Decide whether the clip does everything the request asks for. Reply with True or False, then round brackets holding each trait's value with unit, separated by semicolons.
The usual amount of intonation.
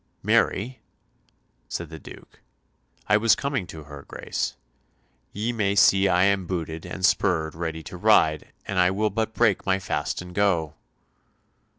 True (4.3 semitones)